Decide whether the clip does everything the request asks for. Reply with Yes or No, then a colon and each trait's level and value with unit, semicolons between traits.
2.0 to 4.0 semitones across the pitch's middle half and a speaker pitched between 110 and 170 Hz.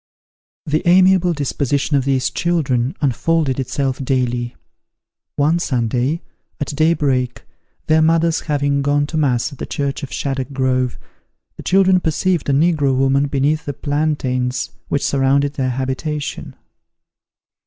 Yes: average, 3.0 semitones; medium, 140 Hz